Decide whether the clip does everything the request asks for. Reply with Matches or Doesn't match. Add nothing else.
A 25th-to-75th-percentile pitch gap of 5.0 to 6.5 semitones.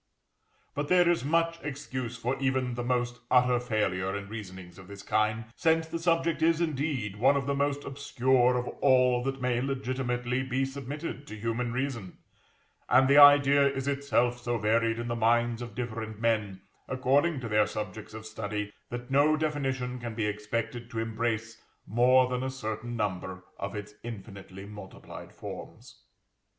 Doesn't match